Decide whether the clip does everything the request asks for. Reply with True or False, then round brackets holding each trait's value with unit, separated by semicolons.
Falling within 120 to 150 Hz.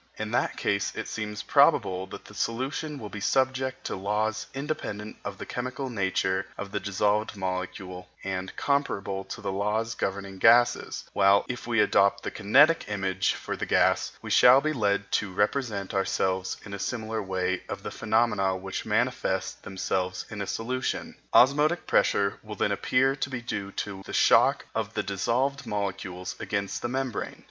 False (105 Hz)